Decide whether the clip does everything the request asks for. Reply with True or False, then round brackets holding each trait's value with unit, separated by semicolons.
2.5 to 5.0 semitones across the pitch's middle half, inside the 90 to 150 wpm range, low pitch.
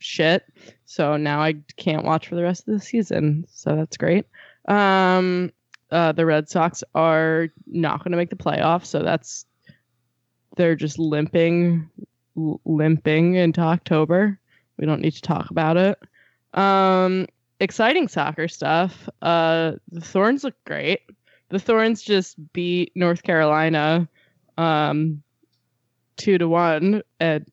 False (2.8 semitones; 135 wpm; 165 Hz)